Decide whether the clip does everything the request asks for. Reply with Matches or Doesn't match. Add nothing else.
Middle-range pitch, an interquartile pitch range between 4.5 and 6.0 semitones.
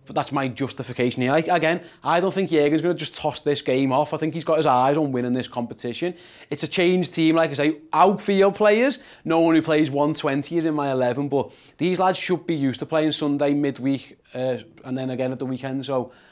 Doesn't match